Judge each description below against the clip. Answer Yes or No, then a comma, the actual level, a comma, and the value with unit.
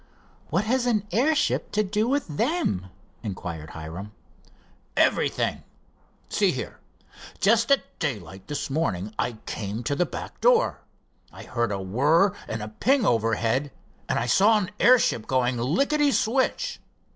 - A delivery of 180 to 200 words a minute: No, average, 140 wpm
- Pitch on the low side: No, medium, 150 Hz